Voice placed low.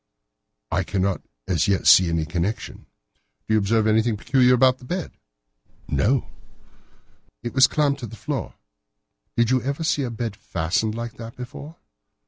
Yes: low, 115 Hz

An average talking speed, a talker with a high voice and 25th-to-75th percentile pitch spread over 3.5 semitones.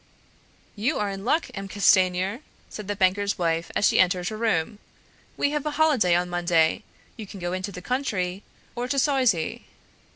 Yes: average, 175 wpm; high, 200 Hz; average, 4.6 semitones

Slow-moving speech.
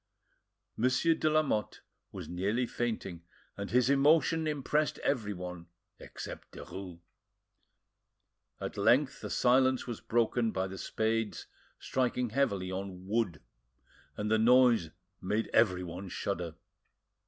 Yes: slow, 110 wpm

